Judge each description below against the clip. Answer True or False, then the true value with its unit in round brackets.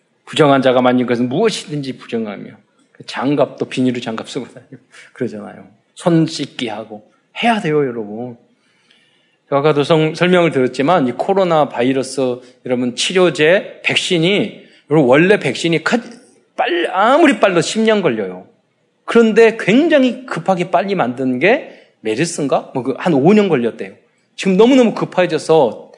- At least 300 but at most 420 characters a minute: True (305 characters per minute)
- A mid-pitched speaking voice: True (160 Hz)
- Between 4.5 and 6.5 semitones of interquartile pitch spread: False (8.0 semitones)